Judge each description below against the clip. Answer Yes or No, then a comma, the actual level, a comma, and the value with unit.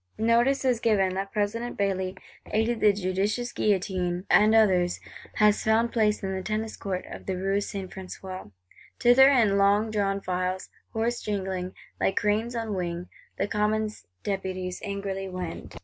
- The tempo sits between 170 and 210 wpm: No, average, 150 wpm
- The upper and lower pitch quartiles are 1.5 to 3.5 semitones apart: Yes, narrow, 2.6 semitones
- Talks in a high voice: Yes, high, 200 Hz